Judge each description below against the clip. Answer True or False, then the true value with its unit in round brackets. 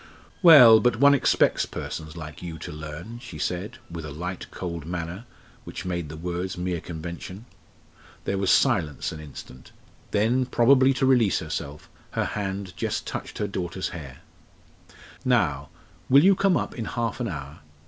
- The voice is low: True (90 Hz)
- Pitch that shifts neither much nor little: False (6.4 semitones)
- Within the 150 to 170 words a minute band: True (160 wpm)